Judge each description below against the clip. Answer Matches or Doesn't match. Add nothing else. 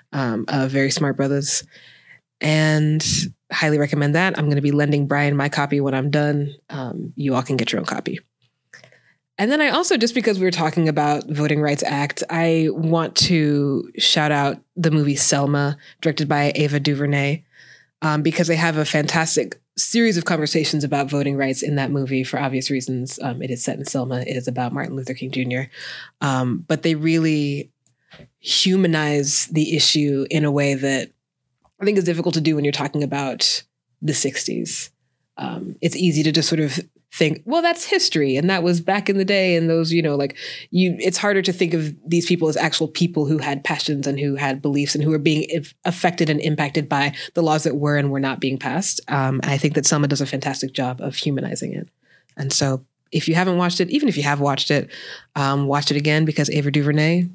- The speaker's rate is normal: Doesn't match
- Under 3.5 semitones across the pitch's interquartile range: Matches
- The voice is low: Doesn't match